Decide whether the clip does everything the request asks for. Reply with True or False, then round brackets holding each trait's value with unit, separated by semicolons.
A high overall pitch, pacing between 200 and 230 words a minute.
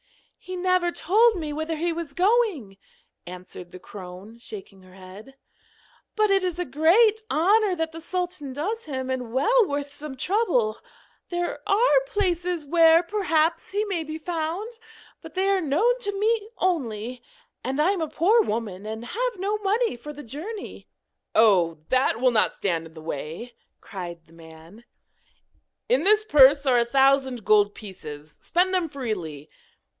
False (305 Hz; 160 wpm)